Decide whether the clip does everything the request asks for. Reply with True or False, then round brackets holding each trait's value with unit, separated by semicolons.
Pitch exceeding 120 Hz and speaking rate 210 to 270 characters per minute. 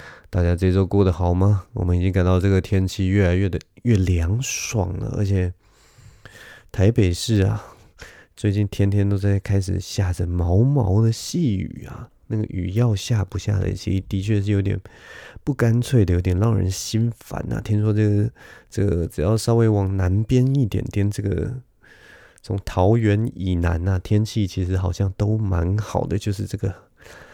False (100 Hz; 250 characters per minute)